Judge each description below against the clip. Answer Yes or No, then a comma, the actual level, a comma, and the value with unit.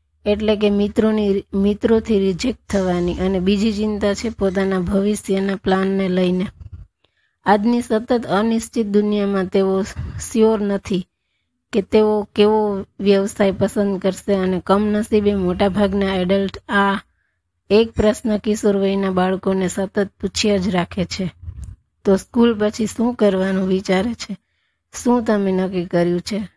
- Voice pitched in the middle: No, high, 200 Hz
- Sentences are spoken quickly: No, average, 120 wpm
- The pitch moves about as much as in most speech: No, narrow, 1.9 semitones